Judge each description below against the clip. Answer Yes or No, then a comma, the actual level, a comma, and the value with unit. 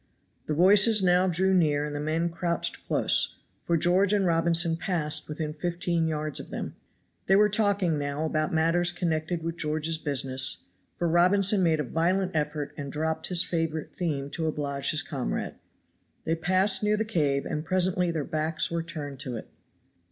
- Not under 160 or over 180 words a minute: Yes, average, 175 wpm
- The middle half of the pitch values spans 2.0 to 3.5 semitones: Yes, average, 2.9 semitones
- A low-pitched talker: No, medium, 165 Hz